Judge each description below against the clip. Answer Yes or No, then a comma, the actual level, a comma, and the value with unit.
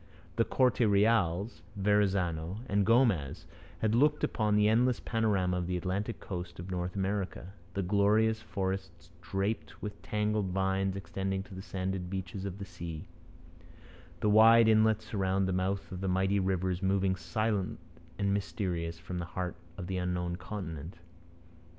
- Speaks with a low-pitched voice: Yes, very low, 95 Hz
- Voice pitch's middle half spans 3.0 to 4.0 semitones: No, narrow, 2.6 semitones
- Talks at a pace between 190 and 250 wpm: No, average, 150 wpm